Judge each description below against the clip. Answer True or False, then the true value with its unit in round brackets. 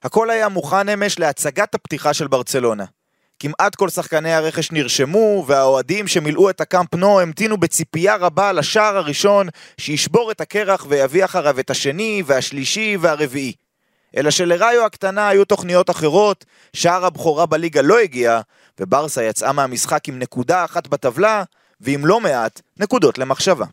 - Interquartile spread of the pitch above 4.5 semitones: True (5.4 semitones)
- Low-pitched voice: False (170 Hz)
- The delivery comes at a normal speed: True (140 wpm)